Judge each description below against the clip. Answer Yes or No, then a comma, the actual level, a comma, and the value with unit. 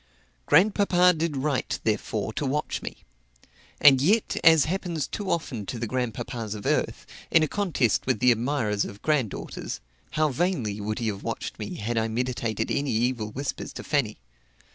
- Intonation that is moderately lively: No, wide, 5.9 semitones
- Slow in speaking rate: No, average, 165 wpm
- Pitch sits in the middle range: No, low, 130 Hz